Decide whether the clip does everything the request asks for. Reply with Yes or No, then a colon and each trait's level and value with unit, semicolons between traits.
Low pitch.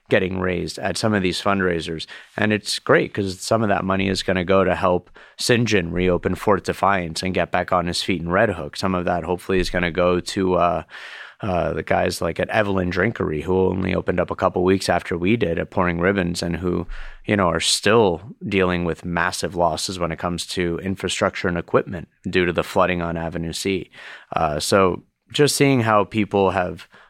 Yes: very low, 90 Hz